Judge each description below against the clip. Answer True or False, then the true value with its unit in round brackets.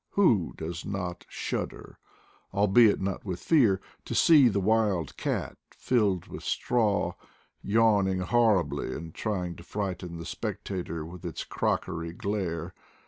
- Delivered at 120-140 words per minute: True (135 wpm)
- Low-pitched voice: True (95 Hz)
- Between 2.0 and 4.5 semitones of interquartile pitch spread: True (3.7 semitones)